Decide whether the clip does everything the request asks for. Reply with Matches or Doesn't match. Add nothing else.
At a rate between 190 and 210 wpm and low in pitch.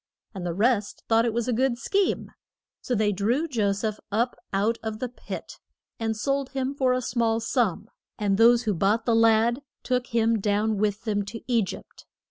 Doesn't match